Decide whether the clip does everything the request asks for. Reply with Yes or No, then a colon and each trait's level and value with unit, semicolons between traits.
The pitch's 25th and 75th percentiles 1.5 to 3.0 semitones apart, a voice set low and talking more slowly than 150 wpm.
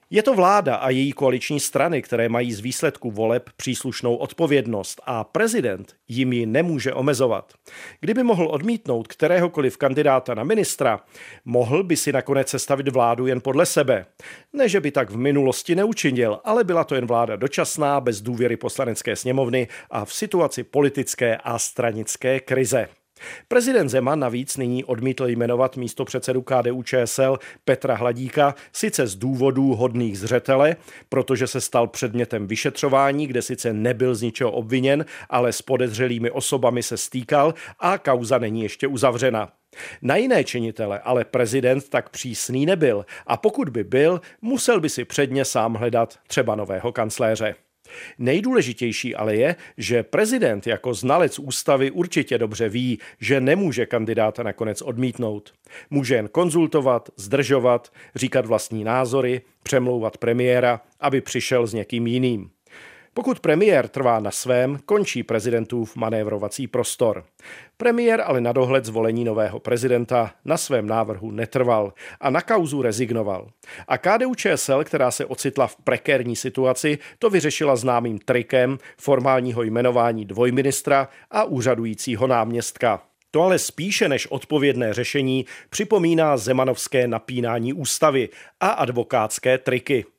Yes: average, 2.7 semitones; low, 130 Hz; average, 135 wpm